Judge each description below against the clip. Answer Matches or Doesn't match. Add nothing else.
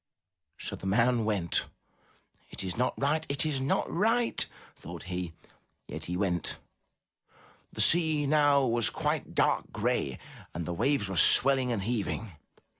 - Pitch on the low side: Matches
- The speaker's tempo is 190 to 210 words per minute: Doesn't match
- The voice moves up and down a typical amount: Doesn't match